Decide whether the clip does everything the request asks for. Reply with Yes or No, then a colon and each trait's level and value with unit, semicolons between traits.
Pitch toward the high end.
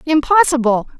Yes: very high, 280 Hz